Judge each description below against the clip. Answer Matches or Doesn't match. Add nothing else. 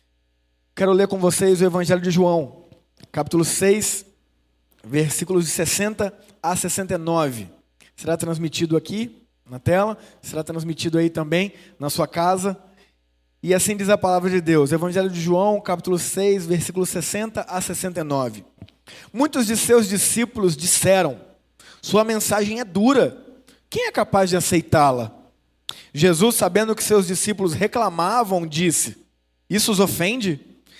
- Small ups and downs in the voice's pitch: Doesn't match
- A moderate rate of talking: Matches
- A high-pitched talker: Doesn't match